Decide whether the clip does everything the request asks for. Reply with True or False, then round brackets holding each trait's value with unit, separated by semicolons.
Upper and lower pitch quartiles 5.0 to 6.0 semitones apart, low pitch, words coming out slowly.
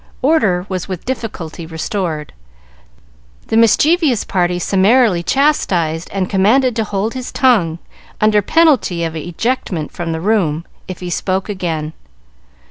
False (5.3 semitones; 190 Hz; 125 wpm)